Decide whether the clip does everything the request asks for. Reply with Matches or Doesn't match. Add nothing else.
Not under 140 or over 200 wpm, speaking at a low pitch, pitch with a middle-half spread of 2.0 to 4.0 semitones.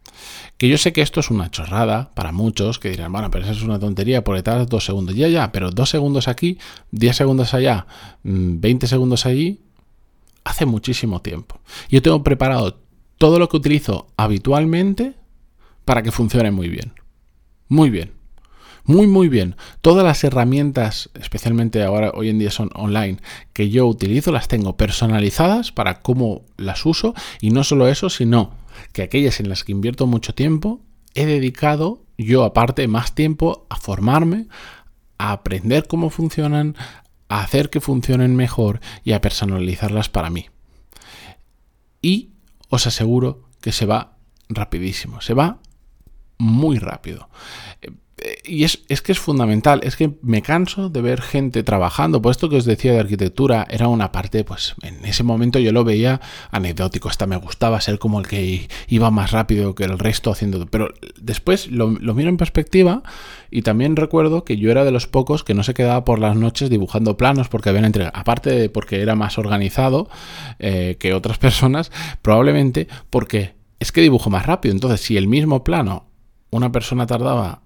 Doesn't match